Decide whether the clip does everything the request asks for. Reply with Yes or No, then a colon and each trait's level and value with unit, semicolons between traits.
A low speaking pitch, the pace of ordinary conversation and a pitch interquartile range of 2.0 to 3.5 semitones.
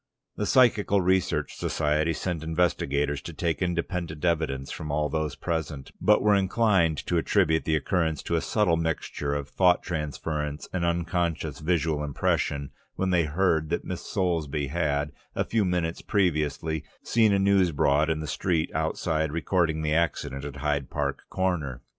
Yes: very low, 80 Hz; average, 160 wpm; average, 3.1 semitones